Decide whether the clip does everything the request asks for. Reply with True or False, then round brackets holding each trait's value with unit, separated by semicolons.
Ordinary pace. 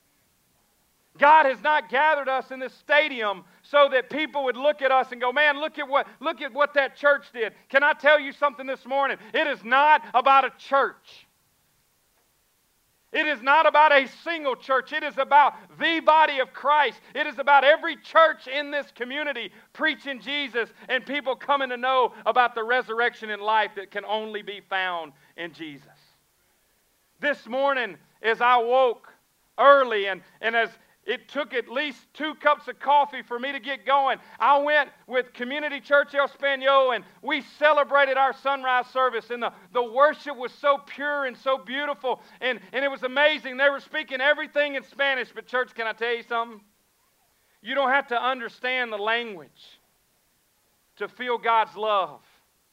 True (175 wpm)